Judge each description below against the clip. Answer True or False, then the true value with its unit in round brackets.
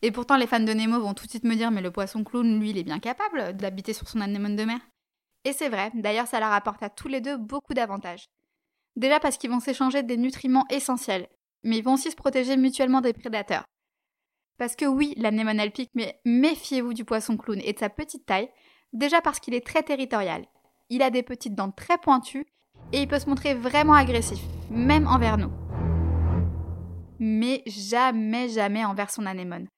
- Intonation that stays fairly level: False (4.6 semitones)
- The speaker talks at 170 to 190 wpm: False (205 wpm)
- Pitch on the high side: True (235 Hz)